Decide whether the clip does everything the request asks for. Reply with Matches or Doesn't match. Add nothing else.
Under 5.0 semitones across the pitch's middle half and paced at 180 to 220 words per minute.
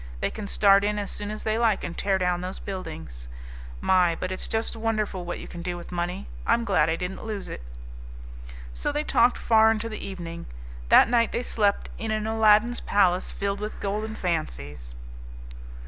Matches